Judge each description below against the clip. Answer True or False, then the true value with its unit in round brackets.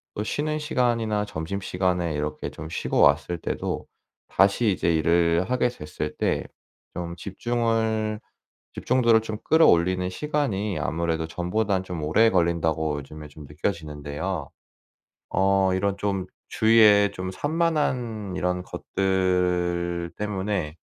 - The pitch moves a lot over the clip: False (4.4 semitones)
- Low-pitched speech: True (95 Hz)